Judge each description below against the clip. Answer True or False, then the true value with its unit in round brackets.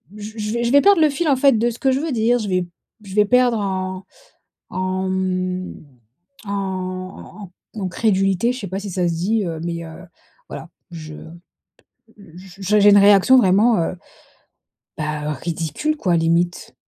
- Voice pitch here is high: True (195 Hz)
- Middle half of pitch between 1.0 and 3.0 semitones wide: False (3.8 semitones)